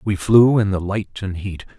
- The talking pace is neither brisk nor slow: No, fast, 235 wpm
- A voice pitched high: No, low, 100 Hz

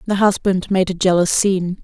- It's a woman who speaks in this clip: Yes, female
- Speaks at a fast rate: No, average, 195 wpm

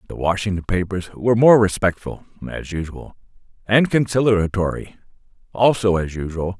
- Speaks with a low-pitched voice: Yes, low, 100 Hz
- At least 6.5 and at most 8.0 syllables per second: No, 5.1 syllables/s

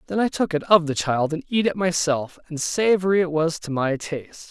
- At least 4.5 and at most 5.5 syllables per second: Yes, 5.3 syllables/s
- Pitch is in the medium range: Yes, medium, 165 Hz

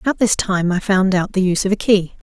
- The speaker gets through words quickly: Yes, fast, 285 wpm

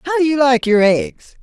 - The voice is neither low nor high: No, high, 235 Hz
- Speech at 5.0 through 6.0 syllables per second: No, 4.0 syllables/s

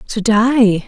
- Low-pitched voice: No, high, 220 Hz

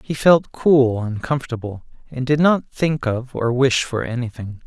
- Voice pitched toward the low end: Yes, low, 130 Hz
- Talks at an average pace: Yes, average, 180 wpm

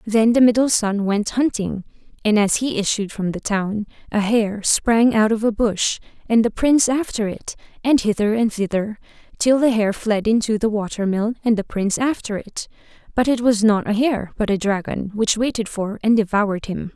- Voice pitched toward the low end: No, high, 215 Hz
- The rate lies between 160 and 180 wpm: No, average, 200 wpm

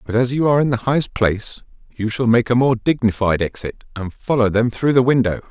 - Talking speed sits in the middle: No, fast, 230 wpm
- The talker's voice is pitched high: No, low, 120 Hz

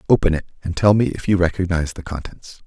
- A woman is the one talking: No, male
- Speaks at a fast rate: Yes, fast, 225 wpm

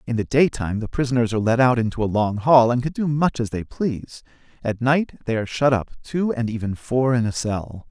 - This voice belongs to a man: Yes, male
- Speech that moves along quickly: Yes, fast, 245 wpm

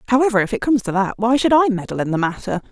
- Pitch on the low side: No, high, 225 Hz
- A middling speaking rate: No, fast, 290 wpm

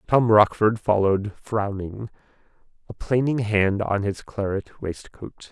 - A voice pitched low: Yes, low, 105 Hz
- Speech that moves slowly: Yes, slow, 120 wpm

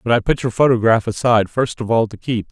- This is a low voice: Yes, low, 115 Hz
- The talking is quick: Yes, fast, 260 wpm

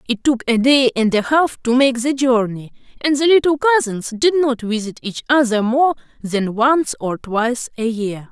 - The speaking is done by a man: No, female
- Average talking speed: Yes, average, 195 wpm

